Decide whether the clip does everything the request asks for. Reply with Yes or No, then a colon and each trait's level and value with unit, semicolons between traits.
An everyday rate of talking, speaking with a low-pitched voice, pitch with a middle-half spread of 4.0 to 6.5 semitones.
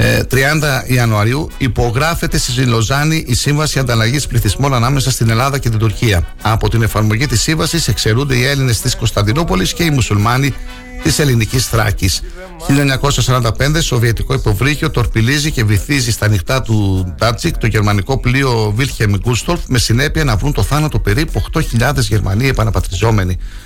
Yes: average, 140 wpm; low, 120 Hz; average, 4.5 semitones